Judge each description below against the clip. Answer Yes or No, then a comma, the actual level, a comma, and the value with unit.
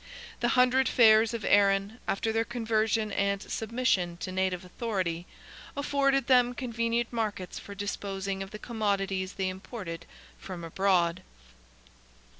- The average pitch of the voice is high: Yes, high, 205 Hz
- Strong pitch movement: No, average, 3.6 semitones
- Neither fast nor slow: No, slow, 115 wpm